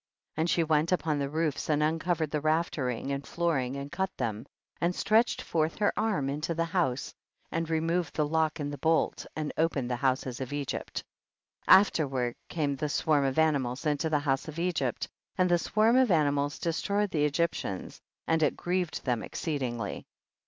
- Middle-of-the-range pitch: Yes, medium, 155 Hz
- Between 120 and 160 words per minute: No, average, 185 wpm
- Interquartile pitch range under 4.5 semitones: Yes, average, 3.3 semitones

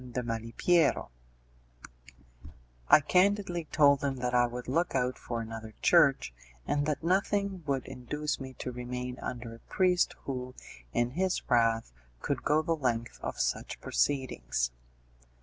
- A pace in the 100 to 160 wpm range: Yes, average, 140 wpm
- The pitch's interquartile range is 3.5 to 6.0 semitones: Yes, average, 4.6 semitones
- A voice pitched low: Yes, low, 130 Hz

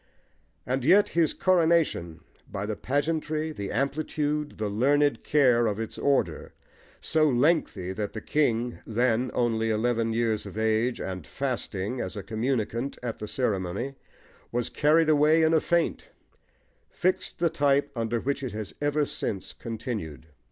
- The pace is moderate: Yes, average, 145 wpm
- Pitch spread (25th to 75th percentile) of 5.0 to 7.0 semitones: Yes, average, 5.3 semitones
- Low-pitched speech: Yes, low, 125 Hz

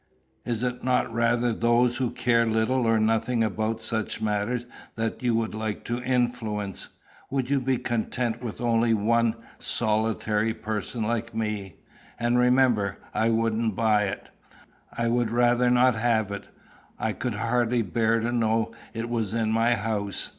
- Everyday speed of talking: Yes, average, 155 wpm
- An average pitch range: No, narrow, 1.6 semitones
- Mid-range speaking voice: No, low, 115 Hz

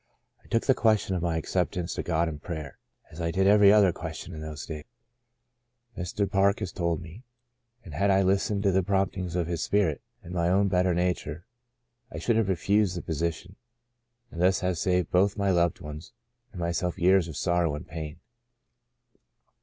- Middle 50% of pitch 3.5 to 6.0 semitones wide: No, average, 2.7 semitones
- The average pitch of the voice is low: Yes, very low, 90 Hz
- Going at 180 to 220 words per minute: Yes, average, 190 wpm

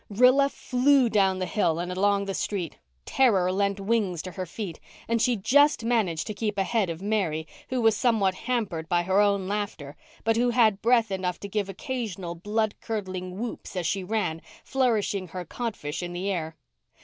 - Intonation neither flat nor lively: Yes, average, 3.8 semitones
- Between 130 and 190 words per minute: Yes, average, 185 wpm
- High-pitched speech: Yes, high, 200 Hz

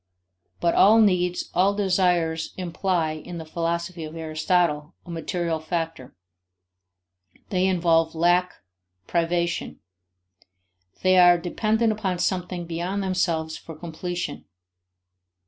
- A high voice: No, medium, 175 Hz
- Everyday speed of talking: No, slow, 105 wpm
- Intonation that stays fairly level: Yes, narrow, 1.9 semitones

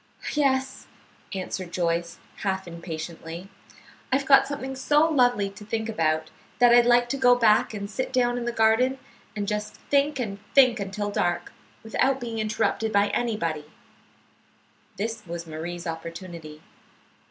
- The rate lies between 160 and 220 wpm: No, average, 140 wpm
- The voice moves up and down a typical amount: No, wide, 6.0 semitones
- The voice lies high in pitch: Yes, high, 215 Hz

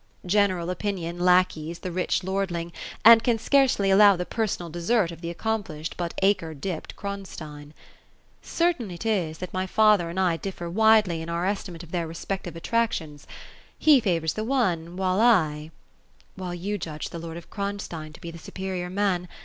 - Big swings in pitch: No, average, 3.3 semitones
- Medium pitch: Yes, medium, 180 Hz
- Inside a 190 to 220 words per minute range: No, average, 180 wpm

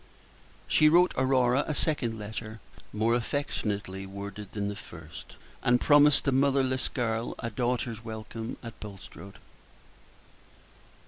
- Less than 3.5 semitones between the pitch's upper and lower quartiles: No, average, 3.9 semitones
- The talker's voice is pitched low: Yes, low, 115 Hz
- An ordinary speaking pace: No, slow, 120 wpm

